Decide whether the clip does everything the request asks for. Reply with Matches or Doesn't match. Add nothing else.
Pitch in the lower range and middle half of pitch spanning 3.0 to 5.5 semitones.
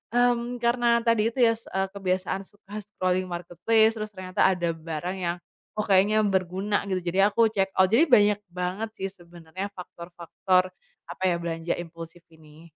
Doesn't match